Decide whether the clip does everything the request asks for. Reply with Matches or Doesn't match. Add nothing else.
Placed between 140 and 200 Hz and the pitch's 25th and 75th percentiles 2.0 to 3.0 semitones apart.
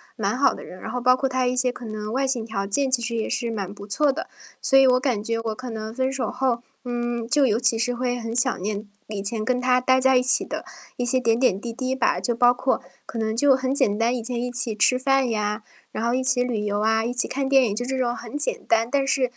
Doesn't match